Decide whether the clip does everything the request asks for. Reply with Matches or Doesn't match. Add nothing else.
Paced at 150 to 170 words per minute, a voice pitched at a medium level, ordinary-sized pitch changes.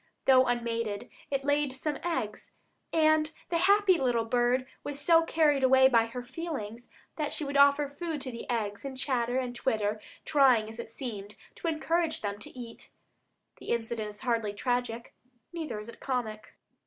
Doesn't match